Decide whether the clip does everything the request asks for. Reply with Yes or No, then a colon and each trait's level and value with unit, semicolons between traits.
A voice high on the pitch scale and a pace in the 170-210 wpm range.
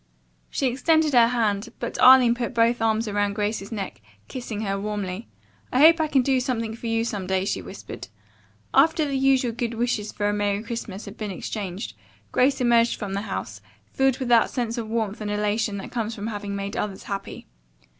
Yes: high, 225 Hz; average, 195 wpm